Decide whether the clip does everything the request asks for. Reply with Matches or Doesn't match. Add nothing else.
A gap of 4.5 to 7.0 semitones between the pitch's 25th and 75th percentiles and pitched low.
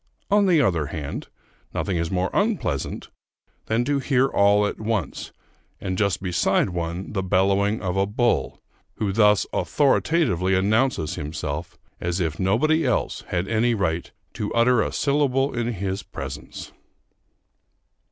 Matches